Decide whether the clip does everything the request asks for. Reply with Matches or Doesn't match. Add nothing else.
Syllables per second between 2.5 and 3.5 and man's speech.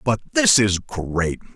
Matches